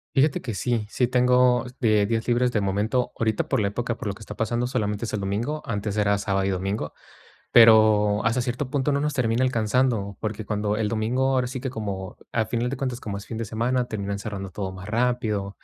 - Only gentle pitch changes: No, average, 3.3 semitones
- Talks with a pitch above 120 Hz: No, low, 110 Hz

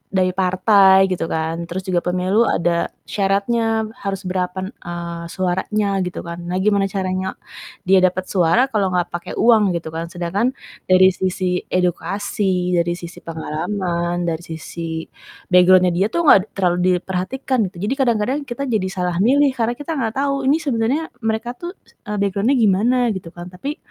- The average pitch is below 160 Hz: No, high, 190 Hz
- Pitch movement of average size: Yes, average, 3.8 semitones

